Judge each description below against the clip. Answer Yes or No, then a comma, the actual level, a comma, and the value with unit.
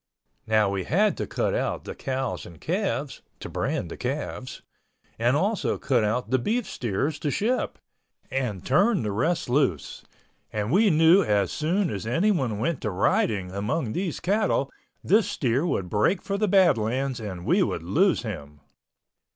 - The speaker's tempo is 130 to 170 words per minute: Yes, average, 165 wpm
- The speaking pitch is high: No, low, 135 Hz